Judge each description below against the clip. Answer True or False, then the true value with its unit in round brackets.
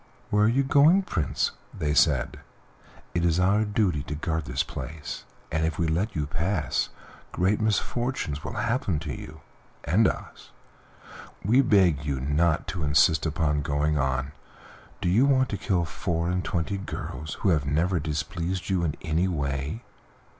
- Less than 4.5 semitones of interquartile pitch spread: False (4.9 semitones)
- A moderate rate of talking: True (165 wpm)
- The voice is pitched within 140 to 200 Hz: False (85 Hz)